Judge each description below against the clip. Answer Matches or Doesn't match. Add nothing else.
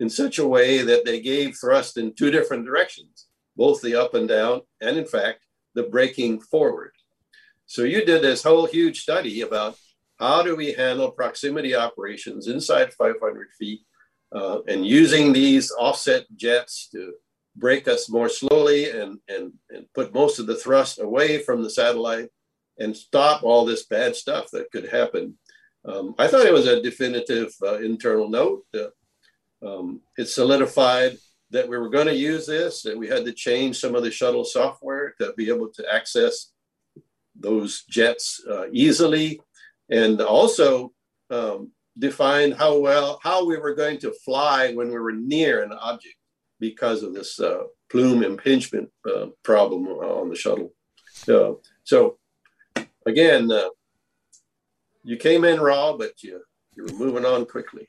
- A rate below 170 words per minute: Matches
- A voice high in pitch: Doesn't match